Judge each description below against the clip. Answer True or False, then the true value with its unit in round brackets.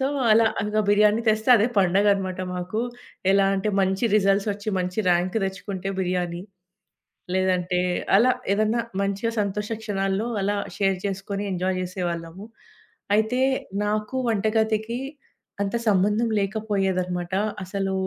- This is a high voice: True (200 Hz)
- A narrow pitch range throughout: True (2.3 semitones)